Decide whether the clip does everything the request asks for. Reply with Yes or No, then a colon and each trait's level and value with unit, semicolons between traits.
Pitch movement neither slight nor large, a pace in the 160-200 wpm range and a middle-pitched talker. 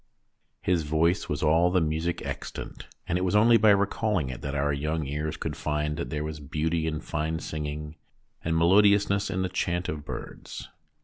No: average, 3.3 semitones; average, 185 wpm; very low, 80 Hz